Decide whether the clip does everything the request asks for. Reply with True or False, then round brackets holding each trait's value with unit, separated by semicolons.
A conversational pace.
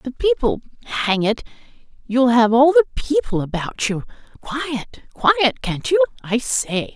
False (110 wpm)